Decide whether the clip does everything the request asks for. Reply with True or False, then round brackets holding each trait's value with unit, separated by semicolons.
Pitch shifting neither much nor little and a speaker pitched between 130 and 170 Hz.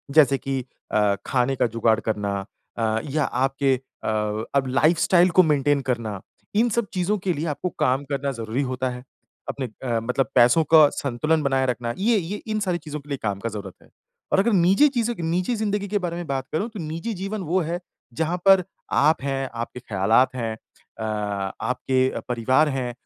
False (6.1 semitones; 140 Hz)